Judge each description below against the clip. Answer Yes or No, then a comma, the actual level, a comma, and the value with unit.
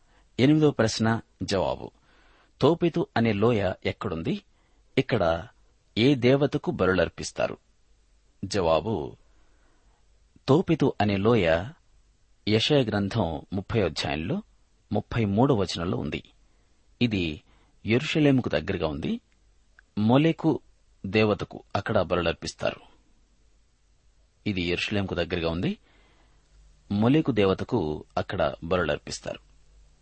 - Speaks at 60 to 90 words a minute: Yes, slow, 70 wpm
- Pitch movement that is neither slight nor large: No, wide, 5.8 semitones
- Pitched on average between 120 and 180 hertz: No, low, 110 Hz